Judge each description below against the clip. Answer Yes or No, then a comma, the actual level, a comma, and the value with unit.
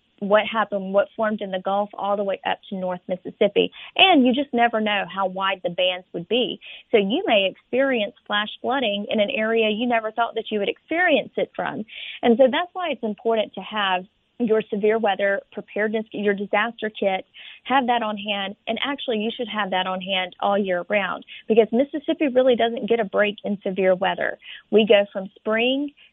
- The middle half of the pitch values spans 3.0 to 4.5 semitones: Yes, average, 3.3 semitones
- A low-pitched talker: No, high, 215 Hz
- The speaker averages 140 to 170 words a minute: No, average, 200 wpm